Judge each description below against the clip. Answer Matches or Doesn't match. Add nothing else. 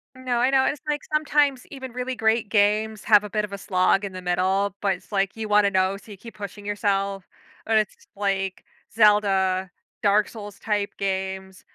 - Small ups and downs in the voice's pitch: Matches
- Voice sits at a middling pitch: Doesn't match